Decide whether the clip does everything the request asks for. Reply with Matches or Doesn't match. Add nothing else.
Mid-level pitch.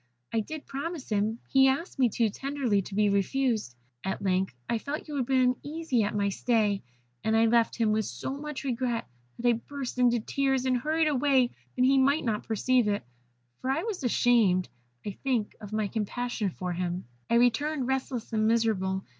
Doesn't match